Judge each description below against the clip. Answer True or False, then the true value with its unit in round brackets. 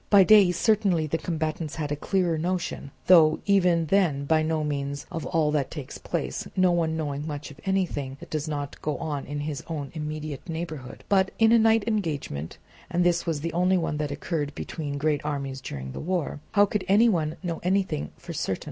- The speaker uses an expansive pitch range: False (3.7 semitones)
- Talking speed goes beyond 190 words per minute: True (200 wpm)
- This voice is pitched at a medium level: True (160 Hz)